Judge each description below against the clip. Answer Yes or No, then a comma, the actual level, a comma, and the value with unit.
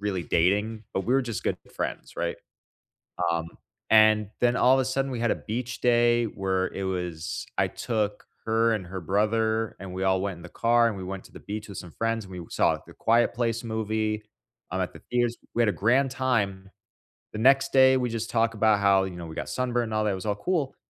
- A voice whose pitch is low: Yes, low, 110 Hz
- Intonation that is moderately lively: Yes, average, 3.5 semitones